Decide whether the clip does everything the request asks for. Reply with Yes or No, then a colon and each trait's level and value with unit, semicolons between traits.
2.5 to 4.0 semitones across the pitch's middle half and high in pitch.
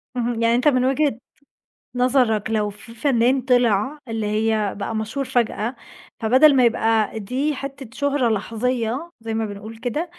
Yes: average, 3.0 semitones; high, 235 Hz